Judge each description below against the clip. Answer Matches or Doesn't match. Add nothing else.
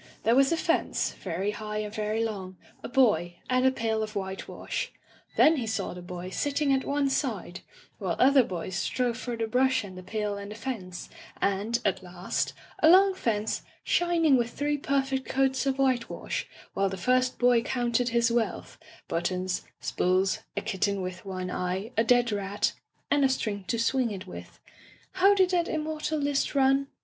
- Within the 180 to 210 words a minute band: Matches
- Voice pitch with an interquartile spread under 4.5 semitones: Doesn't match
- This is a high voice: Matches